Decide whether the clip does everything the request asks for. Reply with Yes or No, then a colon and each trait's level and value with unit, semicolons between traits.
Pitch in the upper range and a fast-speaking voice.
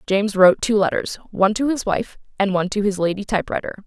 Yes: high, 200 Hz; fast, 220 wpm